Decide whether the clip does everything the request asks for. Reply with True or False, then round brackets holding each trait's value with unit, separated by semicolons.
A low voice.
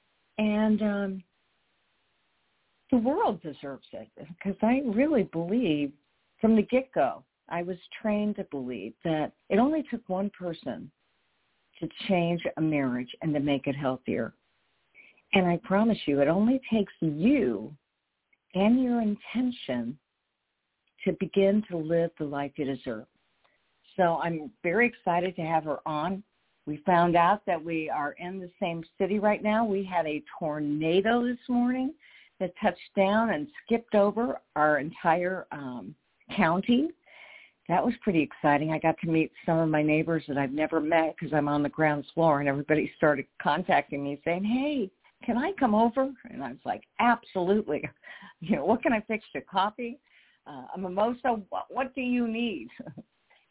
False (185 Hz)